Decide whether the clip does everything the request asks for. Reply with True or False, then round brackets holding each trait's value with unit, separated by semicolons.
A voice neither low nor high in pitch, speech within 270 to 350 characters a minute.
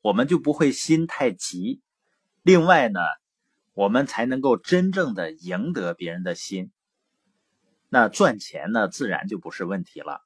False (165 Hz; 215 characters per minute)